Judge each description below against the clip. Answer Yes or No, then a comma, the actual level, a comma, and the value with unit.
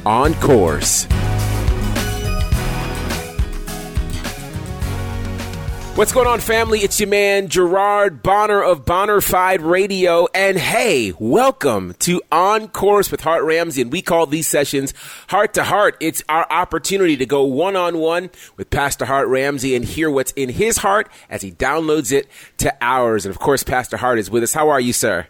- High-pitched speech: No, medium, 140 Hz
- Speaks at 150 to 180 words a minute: Yes, average, 155 wpm